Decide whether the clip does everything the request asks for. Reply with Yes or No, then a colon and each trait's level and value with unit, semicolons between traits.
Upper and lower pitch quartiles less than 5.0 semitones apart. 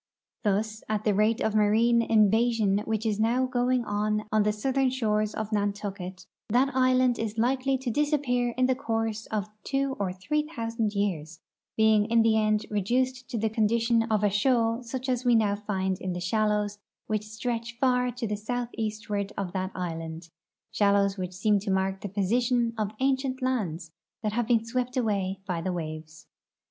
Yes: average, 3.2 semitones